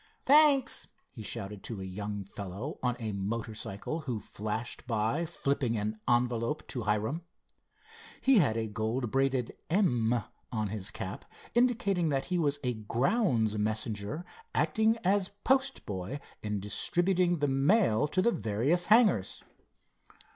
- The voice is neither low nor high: No, low, 120 Hz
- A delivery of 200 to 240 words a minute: No, slow, 135 wpm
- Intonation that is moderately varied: No, wide, 8.3 semitones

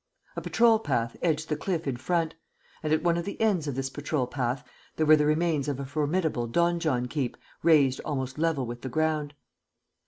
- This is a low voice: No, medium, 150 Hz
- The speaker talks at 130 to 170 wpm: No, average, 195 wpm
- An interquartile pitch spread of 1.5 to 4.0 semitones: Yes, average, 3.7 semitones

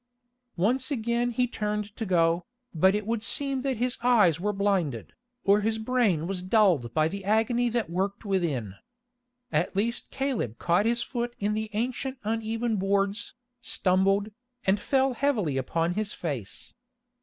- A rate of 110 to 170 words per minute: Yes, average, 155 wpm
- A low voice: No, high, 210 Hz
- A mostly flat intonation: No, average, 4.5 semitones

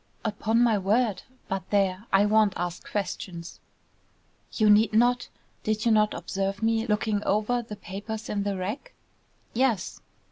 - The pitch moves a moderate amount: No, narrow, 2.3 semitones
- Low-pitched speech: No, high, 210 Hz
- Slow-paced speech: No, average, 145 wpm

